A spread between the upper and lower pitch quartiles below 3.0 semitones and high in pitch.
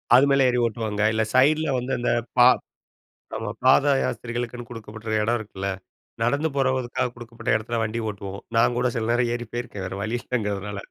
No: narrow, 2.4 semitones; low, 120 Hz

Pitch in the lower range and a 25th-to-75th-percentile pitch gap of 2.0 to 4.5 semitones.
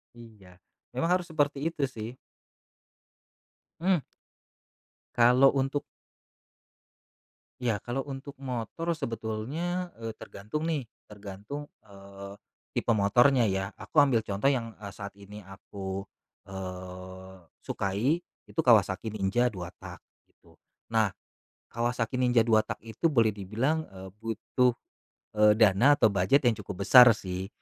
No: low, 115 Hz; average, 5.3 semitones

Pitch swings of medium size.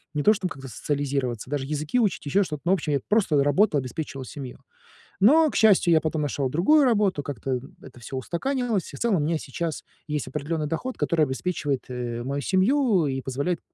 No: wide, 5.8 semitones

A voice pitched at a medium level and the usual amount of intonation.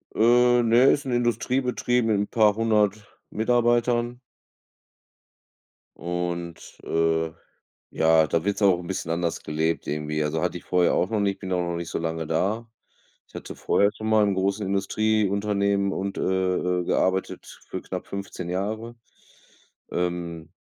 No: low, 100 Hz; average, 4.2 semitones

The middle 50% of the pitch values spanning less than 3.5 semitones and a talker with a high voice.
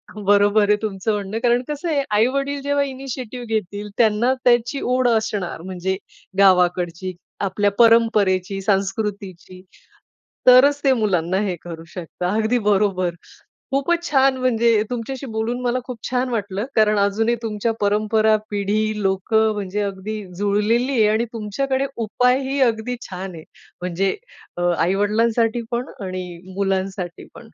No: average, 3.8 semitones; high, 215 Hz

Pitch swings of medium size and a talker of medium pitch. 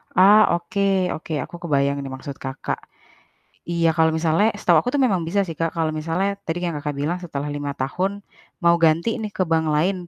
Yes: average, 3.6 semitones; medium, 165 Hz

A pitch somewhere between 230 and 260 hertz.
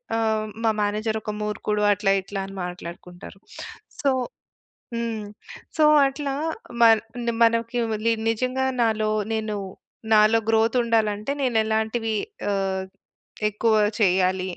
No: high, 220 Hz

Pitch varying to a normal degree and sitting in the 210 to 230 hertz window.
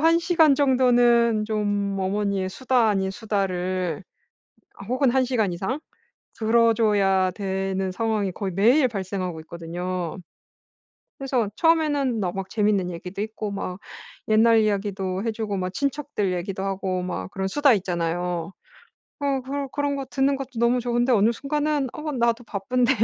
Yes: average, 5.0 semitones; high, 215 Hz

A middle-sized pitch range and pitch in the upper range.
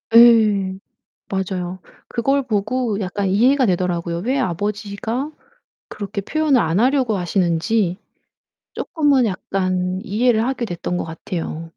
Yes: average, 4.8 semitones; high, 205 Hz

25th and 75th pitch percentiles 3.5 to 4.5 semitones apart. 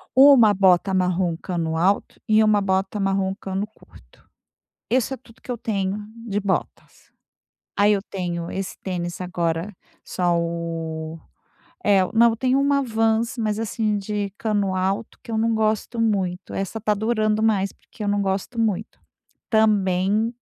No: average, 3.0 semitones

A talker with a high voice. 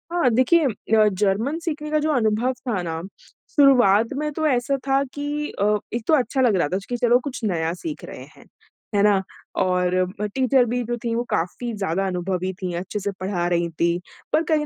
Yes: high, 230 Hz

